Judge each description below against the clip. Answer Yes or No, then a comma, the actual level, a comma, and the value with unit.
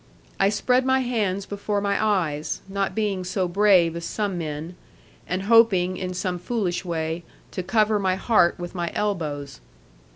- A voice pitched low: No, high, 190 Hz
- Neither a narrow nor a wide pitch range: Yes, average, 3.0 semitones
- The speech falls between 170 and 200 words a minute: No, average, 160 wpm